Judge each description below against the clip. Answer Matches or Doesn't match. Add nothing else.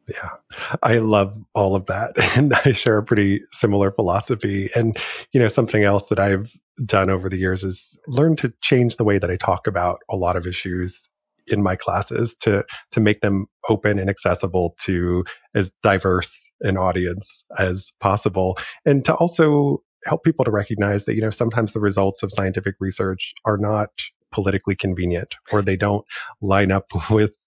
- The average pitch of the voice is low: Matches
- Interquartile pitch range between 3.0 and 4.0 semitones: Doesn't match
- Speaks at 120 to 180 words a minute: Matches